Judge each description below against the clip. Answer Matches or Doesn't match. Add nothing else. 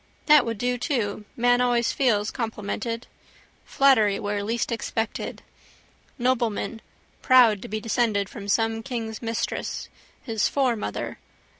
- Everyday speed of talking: Doesn't match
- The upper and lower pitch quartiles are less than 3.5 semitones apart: Matches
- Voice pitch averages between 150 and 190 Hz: Doesn't match